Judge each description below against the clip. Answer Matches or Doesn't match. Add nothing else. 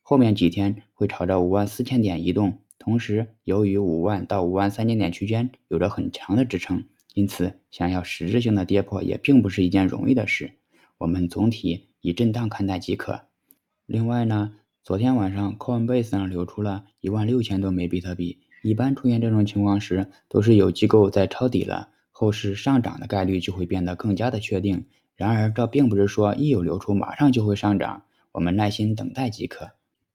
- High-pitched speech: Doesn't match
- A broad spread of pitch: Doesn't match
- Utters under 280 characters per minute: Doesn't match